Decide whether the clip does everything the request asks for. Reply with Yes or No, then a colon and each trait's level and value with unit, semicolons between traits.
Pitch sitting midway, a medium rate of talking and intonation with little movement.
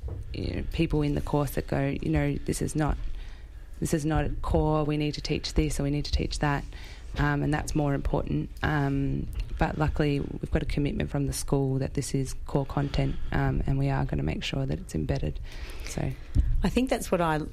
No: medium, 145 Hz; fast, 225 wpm; narrow, 1.8 semitones